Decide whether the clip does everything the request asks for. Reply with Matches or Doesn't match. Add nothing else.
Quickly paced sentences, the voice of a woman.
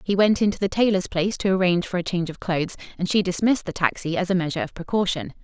Matches